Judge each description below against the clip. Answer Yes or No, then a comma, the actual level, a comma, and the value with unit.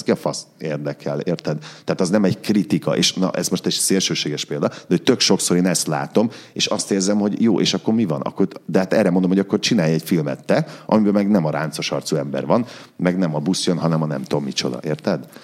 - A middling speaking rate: No, fast, 240 wpm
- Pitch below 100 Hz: Yes, very low, 90 Hz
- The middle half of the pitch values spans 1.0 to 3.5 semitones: No, average, 4.6 semitones